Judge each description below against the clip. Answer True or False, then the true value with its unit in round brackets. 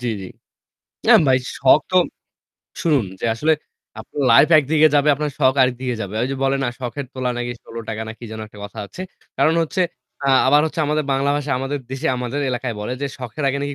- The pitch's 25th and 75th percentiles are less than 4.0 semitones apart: True (3.2 semitones)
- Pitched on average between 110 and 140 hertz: True (135 Hz)